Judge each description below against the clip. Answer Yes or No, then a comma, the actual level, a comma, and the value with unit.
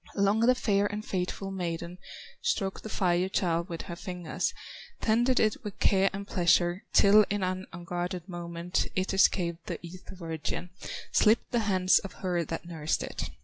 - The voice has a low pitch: No, medium, 185 Hz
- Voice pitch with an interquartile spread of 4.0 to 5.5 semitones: No, narrow, 2.6 semitones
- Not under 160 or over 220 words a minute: Yes, average, 165 wpm